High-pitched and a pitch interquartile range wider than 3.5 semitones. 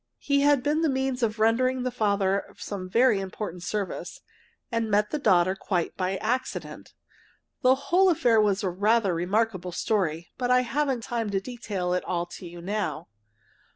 Yes: high, 215 Hz; average, 5.0 semitones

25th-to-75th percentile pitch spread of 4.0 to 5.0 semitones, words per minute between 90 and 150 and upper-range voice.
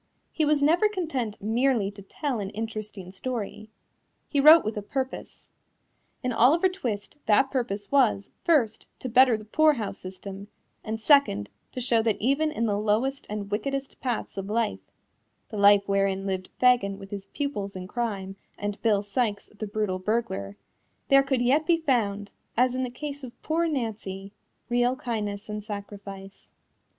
No: average, 4.7 semitones; average, 160 wpm; high, 220 Hz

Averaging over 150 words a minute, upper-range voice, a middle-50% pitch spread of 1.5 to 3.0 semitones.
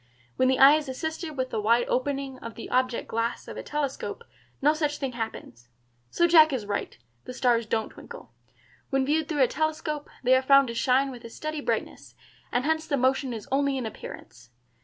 No: average, 200 wpm; very high, 265 Hz; average, 3.6 semitones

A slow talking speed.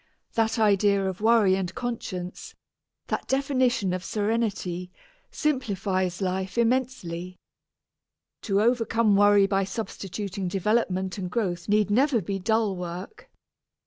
Yes: slow, 110 wpm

